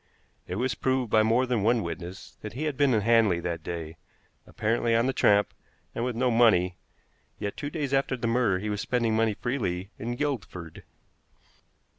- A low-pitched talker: Yes, low, 115 Hz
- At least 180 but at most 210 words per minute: Yes, average, 185 wpm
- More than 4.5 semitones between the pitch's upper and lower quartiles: No, average, 4.2 semitones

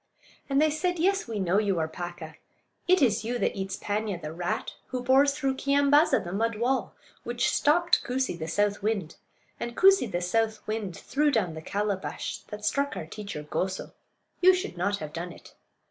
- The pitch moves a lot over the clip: Yes, wide, 6.9 semitones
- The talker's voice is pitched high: Yes, high, 215 Hz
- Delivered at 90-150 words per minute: No, average, 190 wpm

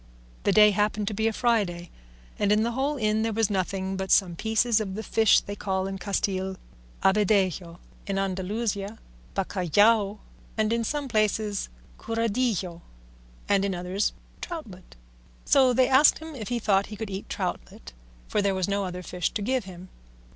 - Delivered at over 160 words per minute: Yes, average, 170 wpm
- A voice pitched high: Yes, high, 205 Hz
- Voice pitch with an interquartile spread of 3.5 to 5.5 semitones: No, average, 2.8 semitones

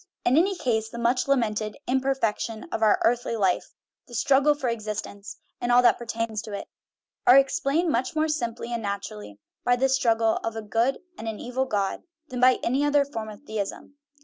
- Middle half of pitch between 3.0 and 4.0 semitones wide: Yes, average, 3.4 semitones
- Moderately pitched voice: No, high, 235 Hz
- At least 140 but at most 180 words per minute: No, average, 195 wpm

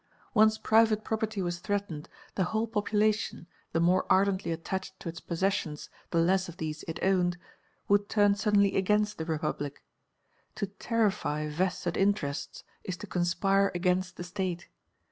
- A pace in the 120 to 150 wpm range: Yes, average, 145 wpm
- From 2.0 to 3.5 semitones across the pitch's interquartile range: Yes, average, 3.1 semitones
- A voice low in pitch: No, high, 190 Hz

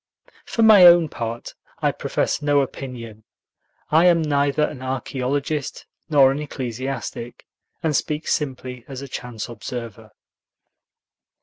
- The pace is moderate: No, slow, 120 wpm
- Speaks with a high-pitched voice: No, low, 135 Hz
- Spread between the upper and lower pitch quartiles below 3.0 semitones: No, average, 3.6 semitones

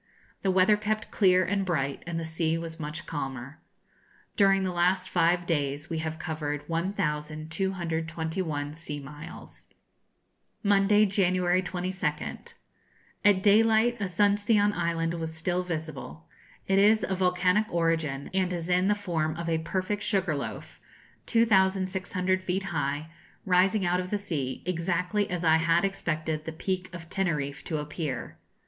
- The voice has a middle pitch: Yes, medium, 175 Hz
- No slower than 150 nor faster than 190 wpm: No, average, 140 wpm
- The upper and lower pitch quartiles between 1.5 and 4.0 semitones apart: Yes, average, 3.1 semitones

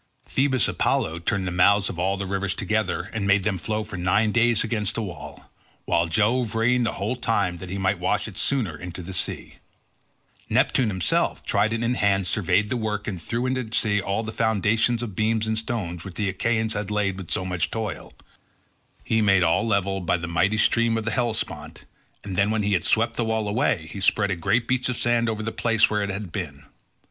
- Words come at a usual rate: No, fast, 215 wpm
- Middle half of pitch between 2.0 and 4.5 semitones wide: Yes, average, 3.1 semitones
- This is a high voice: No, low, 105 Hz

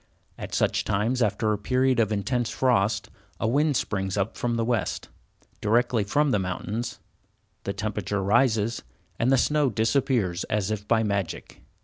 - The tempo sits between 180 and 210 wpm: No, average, 155 wpm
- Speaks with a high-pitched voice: No, low, 110 Hz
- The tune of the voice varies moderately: Yes, average, 3.4 semitones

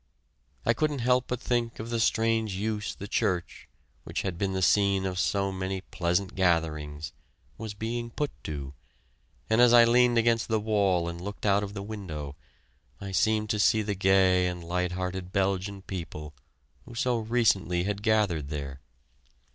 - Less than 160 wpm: No, average, 170 wpm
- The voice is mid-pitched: No, low, 100 Hz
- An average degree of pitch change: Yes, average, 3.7 semitones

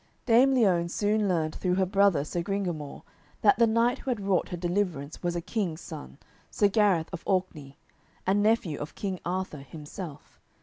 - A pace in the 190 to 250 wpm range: No, average, 175 wpm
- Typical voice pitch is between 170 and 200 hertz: Yes, medium, 185 Hz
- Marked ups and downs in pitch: No, average, 3.8 semitones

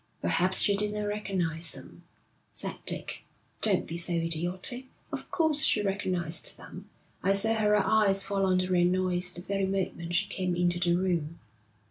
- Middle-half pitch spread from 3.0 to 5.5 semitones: No, narrow, 2.5 semitones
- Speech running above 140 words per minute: Yes, average, 160 wpm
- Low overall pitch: No, medium, 185 Hz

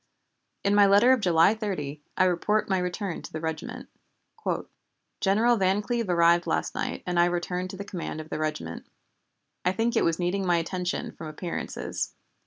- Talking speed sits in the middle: Yes, average, 180 wpm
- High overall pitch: No, medium, 180 Hz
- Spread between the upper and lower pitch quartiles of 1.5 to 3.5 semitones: Yes, average, 3.0 semitones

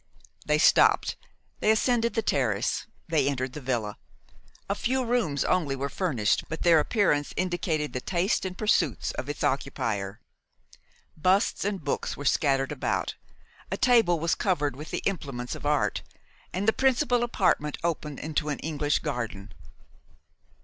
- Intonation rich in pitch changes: Yes, wide, 6.0 semitones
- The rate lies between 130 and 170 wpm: Yes, average, 150 wpm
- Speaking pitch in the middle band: Yes, medium, 155 Hz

